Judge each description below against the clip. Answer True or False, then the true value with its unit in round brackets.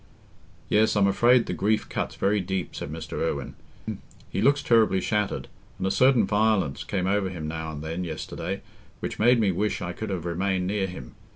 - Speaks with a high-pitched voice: False (95 Hz)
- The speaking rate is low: False (190 wpm)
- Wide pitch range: False (3.7 semitones)